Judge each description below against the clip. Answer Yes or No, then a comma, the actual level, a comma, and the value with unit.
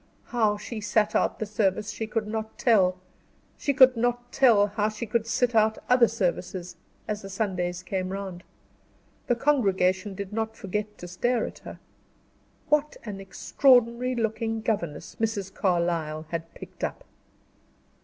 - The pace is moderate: Yes, average, 150 wpm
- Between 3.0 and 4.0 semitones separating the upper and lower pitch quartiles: Yes, average, 3.5 semitones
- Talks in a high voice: Yes, high, 210 Hz